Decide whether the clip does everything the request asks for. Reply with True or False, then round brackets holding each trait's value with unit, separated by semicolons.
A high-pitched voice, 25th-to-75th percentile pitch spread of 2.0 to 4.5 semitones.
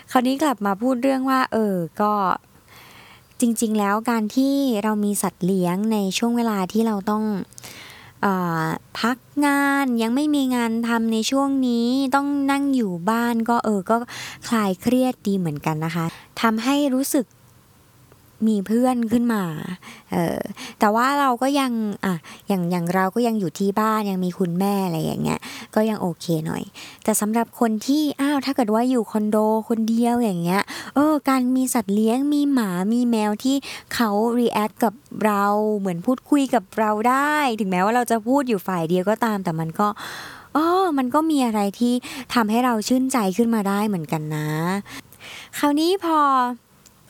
True (225 Hz; 4.2 semitones)